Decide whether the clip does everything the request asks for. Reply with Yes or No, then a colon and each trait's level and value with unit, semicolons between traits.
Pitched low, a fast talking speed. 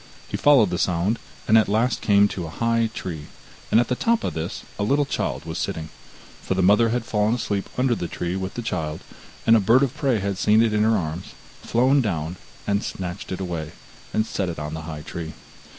Yes: low, 100 Hz; fast, 225 wpm